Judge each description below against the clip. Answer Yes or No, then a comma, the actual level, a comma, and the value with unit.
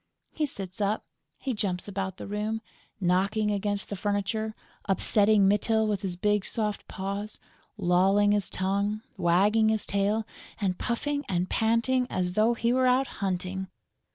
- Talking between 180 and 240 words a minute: No, average, 150 wpm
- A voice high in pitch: Yes, high, 205 Hz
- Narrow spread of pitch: Yes, narrow, 2.2 semitones